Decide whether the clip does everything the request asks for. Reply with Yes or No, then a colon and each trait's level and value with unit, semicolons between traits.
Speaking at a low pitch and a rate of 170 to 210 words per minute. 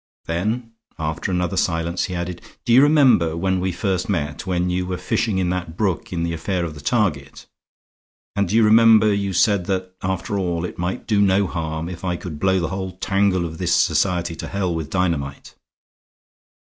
Yes: very low, 90 Hz; average, 195 wpm